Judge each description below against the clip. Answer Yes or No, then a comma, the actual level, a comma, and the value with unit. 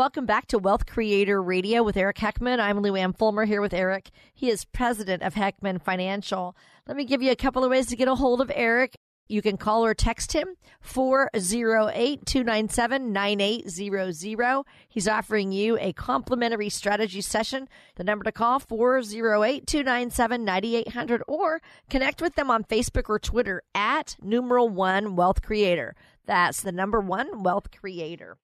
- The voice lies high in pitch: Yes, high, 220 Hz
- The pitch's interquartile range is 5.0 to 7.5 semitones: No, average, 3.8 semitones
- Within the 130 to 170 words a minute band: Yes, average, 155 wpm